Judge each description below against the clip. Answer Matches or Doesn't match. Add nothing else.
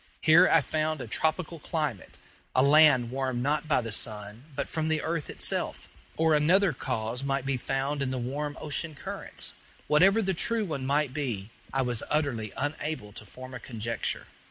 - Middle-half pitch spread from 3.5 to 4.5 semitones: Matches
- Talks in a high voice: Doesn't match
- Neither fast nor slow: Matches